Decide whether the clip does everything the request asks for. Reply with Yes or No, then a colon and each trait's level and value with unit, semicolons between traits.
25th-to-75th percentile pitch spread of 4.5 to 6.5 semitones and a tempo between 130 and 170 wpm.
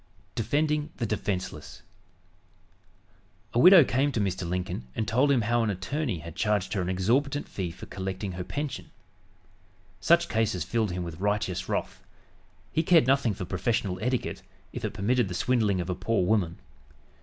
Yes: wide, 5.6 semitones; average, 165 wpm